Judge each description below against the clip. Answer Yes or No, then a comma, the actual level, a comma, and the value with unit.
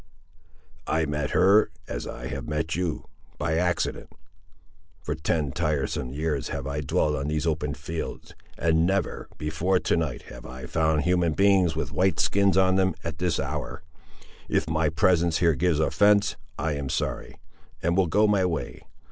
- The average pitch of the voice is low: Yes, very low, 80 Hz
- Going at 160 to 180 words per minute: Yes, average, 165 wpm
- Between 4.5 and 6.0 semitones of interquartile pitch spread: No, average, 3.3 semitones